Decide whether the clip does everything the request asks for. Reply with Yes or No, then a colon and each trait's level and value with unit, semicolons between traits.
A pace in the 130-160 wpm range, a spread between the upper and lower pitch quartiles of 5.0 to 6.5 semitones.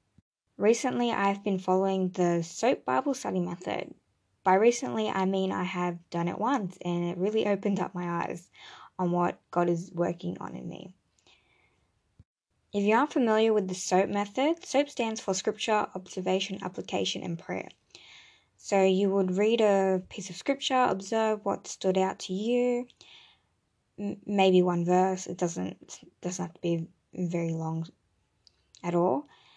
No: average, 155 wpm; average, 3.5 semitones